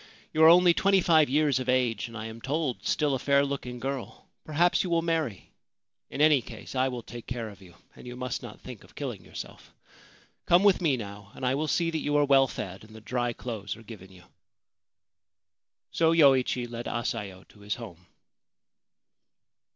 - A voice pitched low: Yes, low, 125 Hz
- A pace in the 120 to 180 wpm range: No, average, 195 wpm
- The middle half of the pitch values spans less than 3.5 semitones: No, average, 5.1 semitones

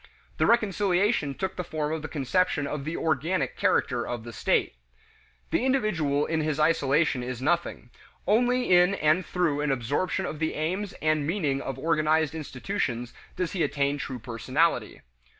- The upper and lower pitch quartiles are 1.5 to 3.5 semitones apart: No, average, 4.4 semitones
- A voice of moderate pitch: Yes, medium, 155 Hz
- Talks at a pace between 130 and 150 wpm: No, average, 160 wpm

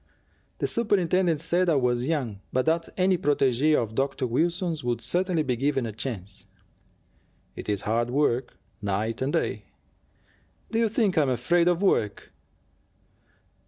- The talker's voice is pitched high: No, medium, 140 Hz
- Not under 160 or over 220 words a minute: No, average, 150 wpm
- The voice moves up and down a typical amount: No, wide, 6.6 semitones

